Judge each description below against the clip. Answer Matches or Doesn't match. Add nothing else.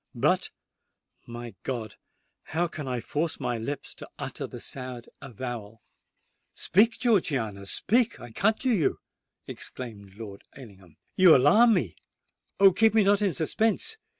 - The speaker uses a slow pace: Matches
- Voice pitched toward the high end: Doesn't match